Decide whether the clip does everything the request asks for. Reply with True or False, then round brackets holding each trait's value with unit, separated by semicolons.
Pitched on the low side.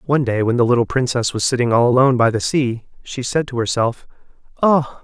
True (125 Hz)